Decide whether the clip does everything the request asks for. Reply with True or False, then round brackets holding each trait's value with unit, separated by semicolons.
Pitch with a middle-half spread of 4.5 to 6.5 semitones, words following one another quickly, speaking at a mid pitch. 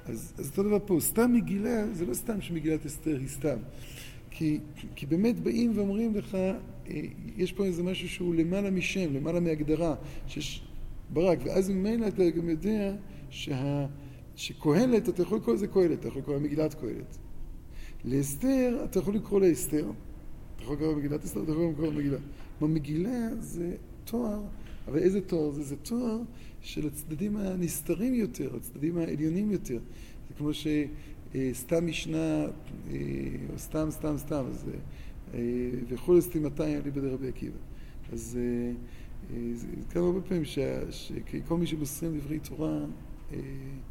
False (5.4 semitones; 140 wpm; 155 Hz)